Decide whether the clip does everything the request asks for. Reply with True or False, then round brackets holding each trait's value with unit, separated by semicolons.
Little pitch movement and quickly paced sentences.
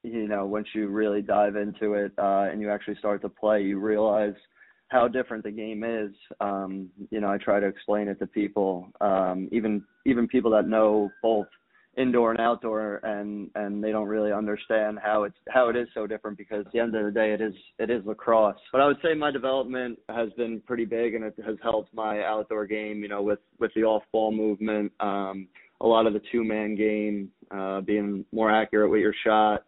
True (1.4 semitones; 215 wpm)